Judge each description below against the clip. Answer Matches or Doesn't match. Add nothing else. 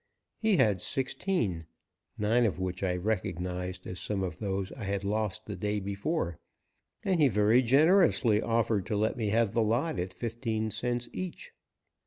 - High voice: Doesn't match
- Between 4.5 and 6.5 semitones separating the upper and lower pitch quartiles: Doesn't match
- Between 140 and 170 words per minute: Matches